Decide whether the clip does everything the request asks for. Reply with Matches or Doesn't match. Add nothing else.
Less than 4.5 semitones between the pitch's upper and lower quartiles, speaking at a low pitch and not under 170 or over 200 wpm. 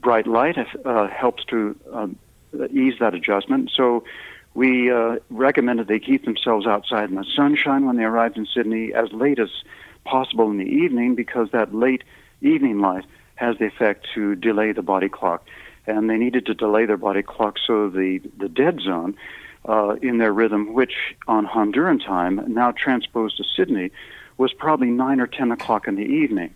Matches